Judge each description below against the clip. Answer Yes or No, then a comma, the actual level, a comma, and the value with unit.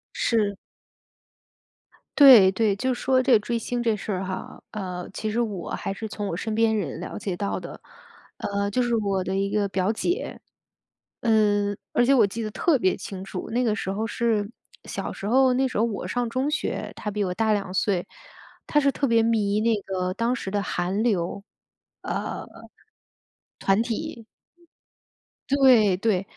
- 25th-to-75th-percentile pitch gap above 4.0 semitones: No, average, 3.2 semitones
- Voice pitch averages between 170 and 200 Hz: No, high, 215 Hz